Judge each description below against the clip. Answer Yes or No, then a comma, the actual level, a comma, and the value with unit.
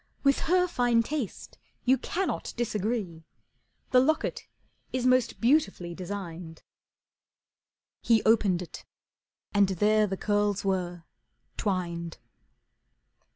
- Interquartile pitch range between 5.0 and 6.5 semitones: Yes, wide, 5.4 semitones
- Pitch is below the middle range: No, high, 210 Hz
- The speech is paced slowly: Yes, slow, 100 wpm